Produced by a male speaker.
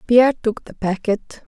No: female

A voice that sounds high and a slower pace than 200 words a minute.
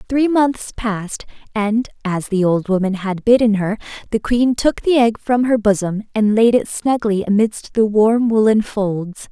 Yes: high, 220 Hz; average, 180 wpm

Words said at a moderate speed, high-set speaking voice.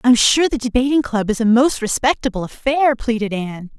Yes: average, 190 wpm; high, 240 Hz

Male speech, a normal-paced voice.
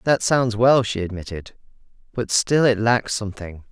Yes: male; average, 160 wpm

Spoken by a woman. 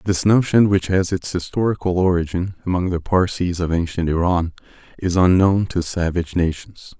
No: male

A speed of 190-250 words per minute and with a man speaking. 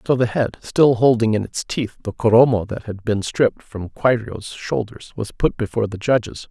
Yes: fast, 205 wpm; male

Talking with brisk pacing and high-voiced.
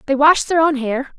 Yes: fast, 255 wpm; very high, 285 Hz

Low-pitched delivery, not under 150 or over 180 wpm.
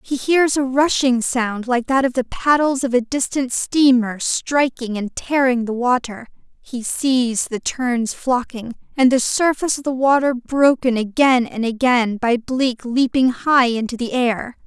No: very high, 250 Hz; average, 170 wpm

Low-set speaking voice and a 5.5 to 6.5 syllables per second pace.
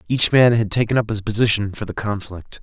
Yes: low, 110 Hz; 5.7 syllables/s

